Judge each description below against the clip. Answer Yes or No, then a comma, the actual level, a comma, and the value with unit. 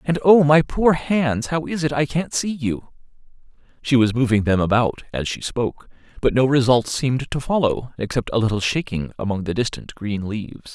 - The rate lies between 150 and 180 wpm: No, average, 195 wpm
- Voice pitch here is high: No, low, 130 Hz